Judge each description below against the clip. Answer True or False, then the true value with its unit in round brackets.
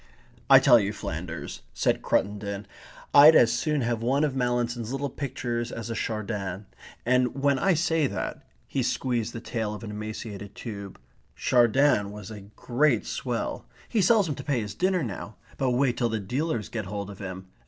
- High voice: False (120 Hz)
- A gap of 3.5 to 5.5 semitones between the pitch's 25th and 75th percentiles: True (4.5 semitones)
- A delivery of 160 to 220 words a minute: True (185 wpm)